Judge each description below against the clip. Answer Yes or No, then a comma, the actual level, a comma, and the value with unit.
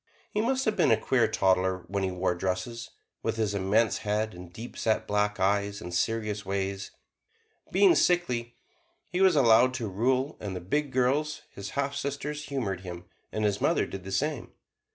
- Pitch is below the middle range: Yes, low, 110 Hz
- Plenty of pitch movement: Yes, wide, 5.8 semitones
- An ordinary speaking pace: Yes, average, 180 wpm